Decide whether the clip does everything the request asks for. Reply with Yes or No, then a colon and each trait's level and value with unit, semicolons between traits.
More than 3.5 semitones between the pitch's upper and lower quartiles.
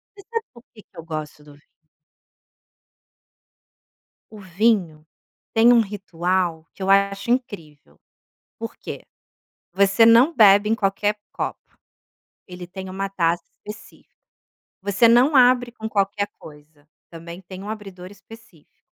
Yes: average, 4.4 semitones